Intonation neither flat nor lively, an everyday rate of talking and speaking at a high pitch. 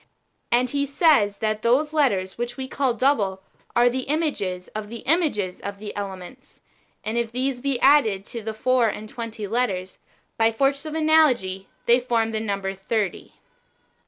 Yes: average, 4.7 semitones; average, 170 wpm; high, 230 Hz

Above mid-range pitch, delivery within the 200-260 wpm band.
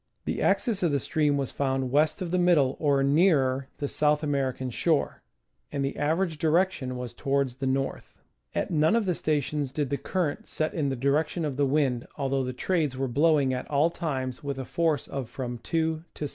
No: medium, 145 Hz; fast, 205 wpm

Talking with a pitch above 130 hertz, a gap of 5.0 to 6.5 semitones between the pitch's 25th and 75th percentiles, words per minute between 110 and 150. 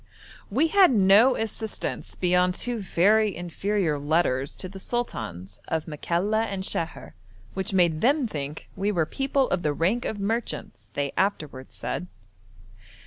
Yes: high, 190 Hz; wide, 5.4 semitones; average, 140 wpm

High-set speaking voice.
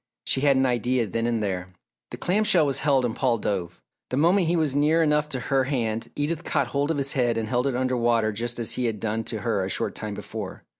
No: low, 125 Hz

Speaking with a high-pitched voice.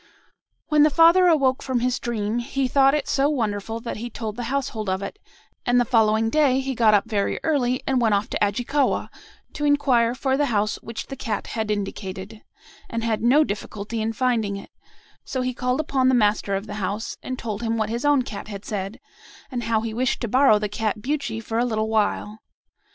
Yes: high, 230 Hz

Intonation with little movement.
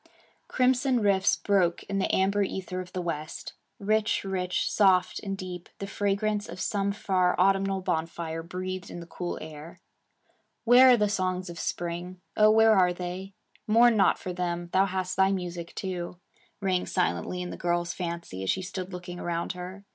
Yes: narrow, 2.1 semitones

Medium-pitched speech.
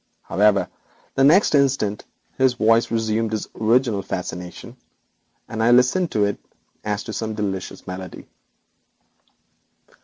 No: low, 110 Hz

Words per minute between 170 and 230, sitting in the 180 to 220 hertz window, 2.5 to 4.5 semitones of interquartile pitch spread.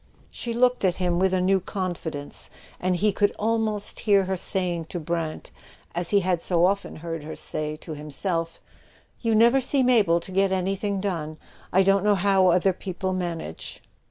Yes: average, 180 wpm; medium, 185 Hz; average, 2.8 semitones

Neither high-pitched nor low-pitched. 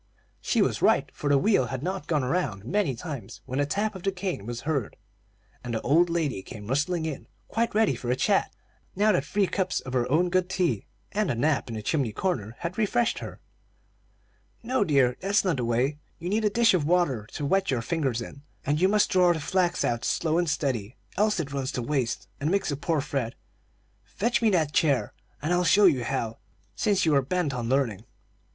Yes: medium, 150 Hz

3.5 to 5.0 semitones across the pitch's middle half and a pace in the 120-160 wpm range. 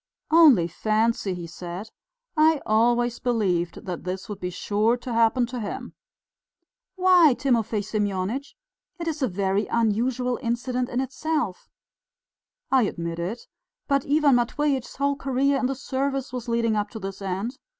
Yes: average, 4.7 semitones; average, 150 wpm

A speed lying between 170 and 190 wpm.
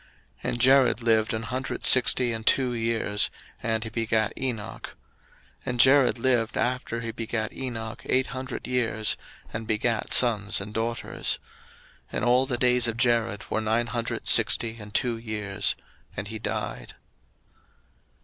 No: average, 155 wpm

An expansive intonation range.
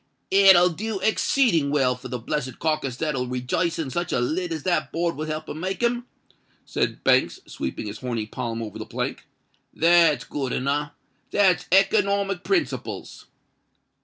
Yes: wide, 6.5 semitones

